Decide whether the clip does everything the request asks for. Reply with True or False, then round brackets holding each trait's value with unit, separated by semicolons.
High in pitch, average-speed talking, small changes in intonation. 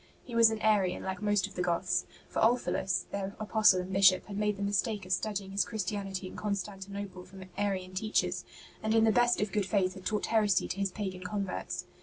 False (200 Hz; 210 wpm; 2.0 semitones)